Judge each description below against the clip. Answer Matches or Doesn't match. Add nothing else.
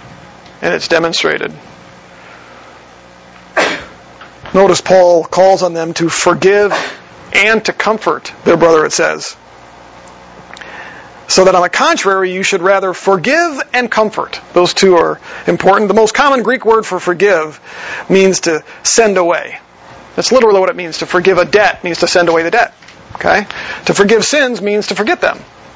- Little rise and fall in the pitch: Doesn't match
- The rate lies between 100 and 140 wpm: Doesn't match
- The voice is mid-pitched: Matches